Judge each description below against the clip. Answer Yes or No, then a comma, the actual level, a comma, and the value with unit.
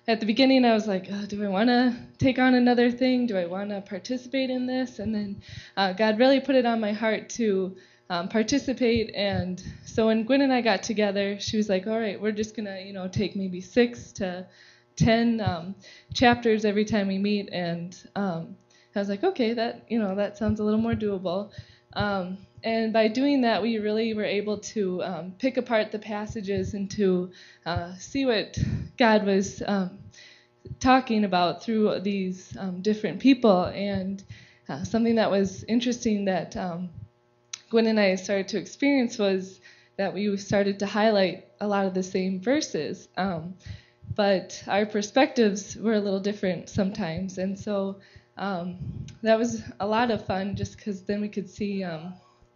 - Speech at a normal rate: Yes, average, 185 wpm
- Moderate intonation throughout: Yes, average, 3.0 semitones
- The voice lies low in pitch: No, high, 205 Hz